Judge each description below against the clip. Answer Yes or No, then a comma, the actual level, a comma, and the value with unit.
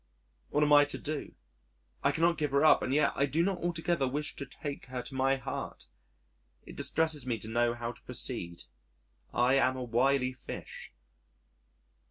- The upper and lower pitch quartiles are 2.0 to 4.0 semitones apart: Yes, average, 2.9 semitones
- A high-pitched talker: No, low, 135 Hz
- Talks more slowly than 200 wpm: Yes, average, 180 wpm